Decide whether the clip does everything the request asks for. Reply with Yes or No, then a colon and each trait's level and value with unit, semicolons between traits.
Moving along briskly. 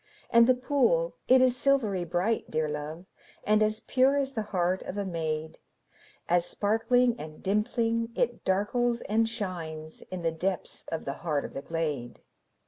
No: average, 165 wpm